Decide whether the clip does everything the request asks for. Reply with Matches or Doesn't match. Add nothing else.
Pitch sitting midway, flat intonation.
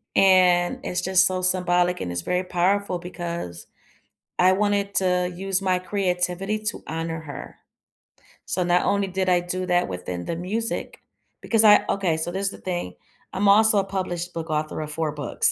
Matches